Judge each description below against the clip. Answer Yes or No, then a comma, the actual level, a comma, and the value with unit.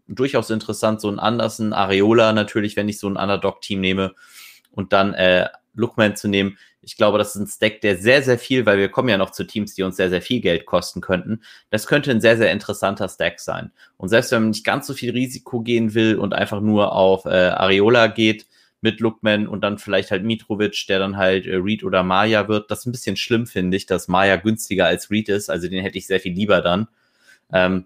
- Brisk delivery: Yes, fast, 230 wpm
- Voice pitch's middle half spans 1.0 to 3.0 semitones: Yes, narrow, 2.4 semitones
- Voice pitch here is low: Yes, low, 105 Hz